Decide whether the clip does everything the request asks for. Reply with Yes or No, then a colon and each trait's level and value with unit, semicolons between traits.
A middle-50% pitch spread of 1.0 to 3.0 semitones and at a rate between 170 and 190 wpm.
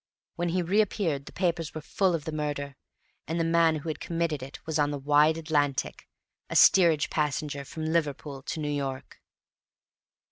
Yes: narrow, 2.5 semitones; average, 175 wpm